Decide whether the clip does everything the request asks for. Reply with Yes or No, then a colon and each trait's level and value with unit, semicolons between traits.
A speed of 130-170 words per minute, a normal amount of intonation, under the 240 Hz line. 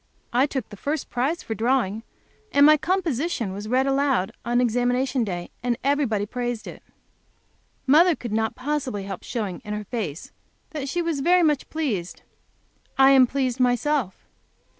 No: average, 160 wpm; average, 4.5 semitones; very high, 255 Hz